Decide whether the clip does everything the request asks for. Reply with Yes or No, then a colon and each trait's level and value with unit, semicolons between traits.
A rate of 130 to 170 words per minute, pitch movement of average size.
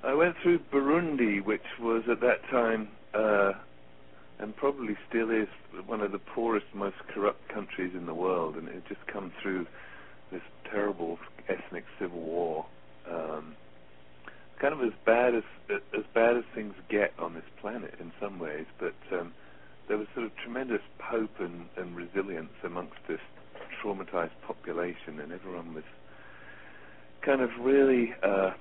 No: average, 155 wpm; wide, 7.0 semitones